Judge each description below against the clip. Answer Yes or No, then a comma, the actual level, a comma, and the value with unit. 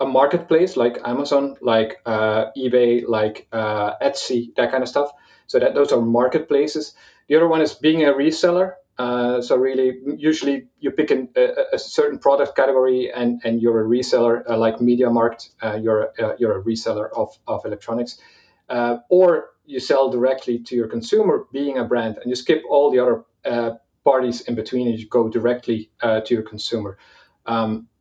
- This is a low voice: Yes, low, 125 Hz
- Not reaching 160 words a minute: No, average, 185 wpm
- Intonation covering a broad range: No, average, 3.8 semitones